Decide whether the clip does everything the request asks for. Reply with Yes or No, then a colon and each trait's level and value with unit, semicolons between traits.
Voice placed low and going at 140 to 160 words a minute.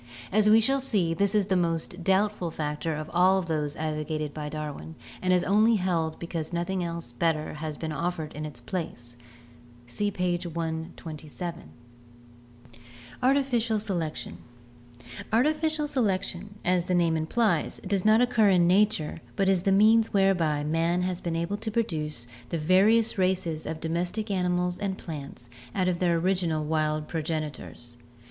No: medium, 175 Hz; average, 155 wpm